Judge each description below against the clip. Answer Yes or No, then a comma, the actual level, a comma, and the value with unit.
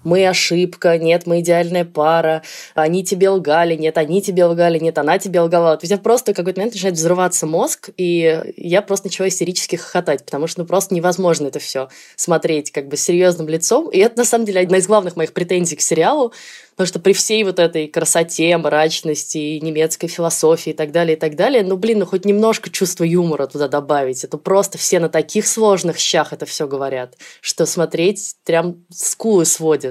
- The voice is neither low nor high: Yes, medium, 170 Hz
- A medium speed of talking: No, fast, 195 wpm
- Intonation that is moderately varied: Yes, average, 3.0 semitones